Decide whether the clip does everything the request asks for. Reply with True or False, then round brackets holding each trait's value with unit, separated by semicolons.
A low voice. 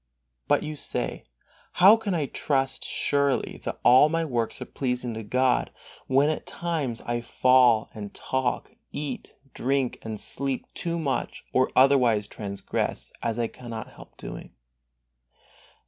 True (130 Hz)